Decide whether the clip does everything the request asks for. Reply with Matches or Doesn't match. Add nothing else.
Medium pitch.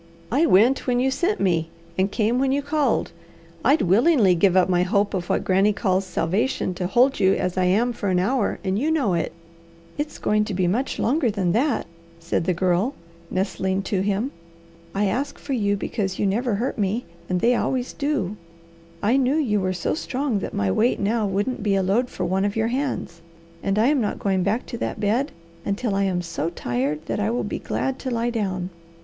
Doesn't match